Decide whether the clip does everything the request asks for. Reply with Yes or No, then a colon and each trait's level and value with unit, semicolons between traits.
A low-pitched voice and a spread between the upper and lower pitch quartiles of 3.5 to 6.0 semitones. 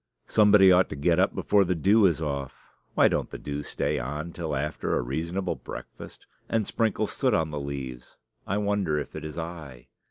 Yes: very low, 80 Hz; average, 5.2 semitones